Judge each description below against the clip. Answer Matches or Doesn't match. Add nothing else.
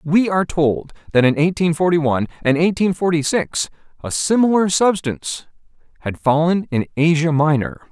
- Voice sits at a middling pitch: Matches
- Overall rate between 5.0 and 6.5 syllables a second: Matches